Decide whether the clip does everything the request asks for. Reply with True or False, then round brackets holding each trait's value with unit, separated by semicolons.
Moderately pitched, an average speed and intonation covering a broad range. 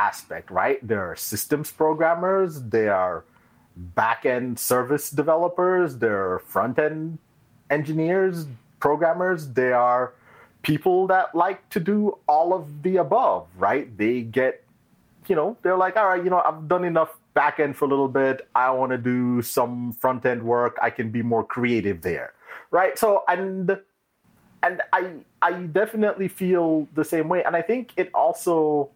True (155 Hz; 155 wpm; 6.4 semitones)